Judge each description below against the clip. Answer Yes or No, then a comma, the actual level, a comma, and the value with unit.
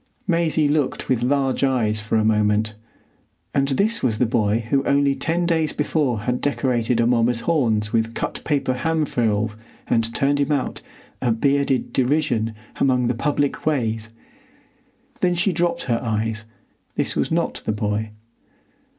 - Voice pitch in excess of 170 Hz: No, low, 125 Hz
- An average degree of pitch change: Yes, average, 4.4 semitones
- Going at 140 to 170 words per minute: Yes, average, 150 wpm